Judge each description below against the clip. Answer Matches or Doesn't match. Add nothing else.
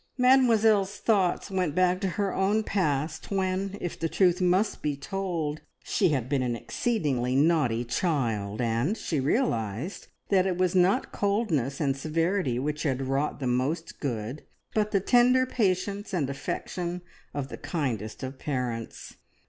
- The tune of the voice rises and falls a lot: Matches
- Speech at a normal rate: Matches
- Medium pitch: Matches